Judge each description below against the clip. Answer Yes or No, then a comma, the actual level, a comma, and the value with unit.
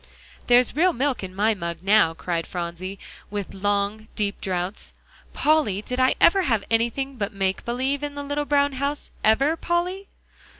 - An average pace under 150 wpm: No, average, 165 wpm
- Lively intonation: Yes, wide, 6.4 semitones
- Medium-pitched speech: No, high, 225 Hz